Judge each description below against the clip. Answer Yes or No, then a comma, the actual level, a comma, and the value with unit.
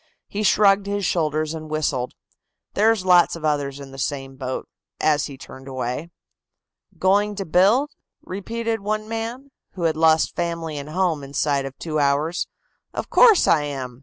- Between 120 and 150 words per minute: No, average, 165 wpm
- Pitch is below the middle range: No, medium, 160 Hz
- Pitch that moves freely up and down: Yes, wide, 6.0 semitones